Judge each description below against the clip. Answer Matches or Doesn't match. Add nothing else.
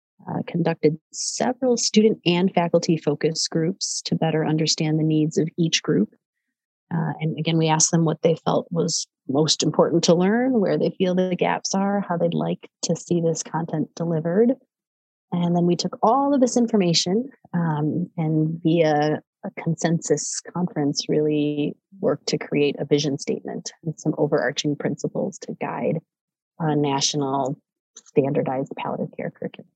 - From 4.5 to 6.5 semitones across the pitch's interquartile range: Doesn't match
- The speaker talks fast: Doesn't match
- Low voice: Doesn't match